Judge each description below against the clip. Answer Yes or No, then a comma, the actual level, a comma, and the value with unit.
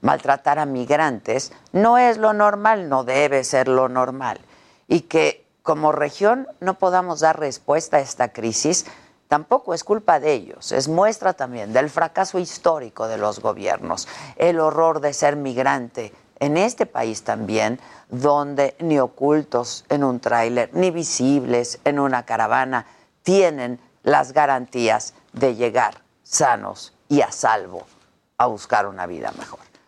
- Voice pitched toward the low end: No, medium, 145 Hz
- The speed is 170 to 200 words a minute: No, average, 145 wpm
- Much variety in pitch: No, average, 4.9 semitones